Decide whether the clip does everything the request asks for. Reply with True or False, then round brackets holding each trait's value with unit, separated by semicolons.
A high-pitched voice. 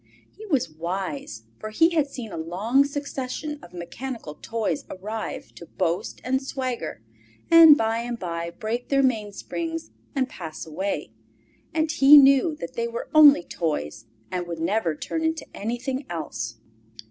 True (235 Hz)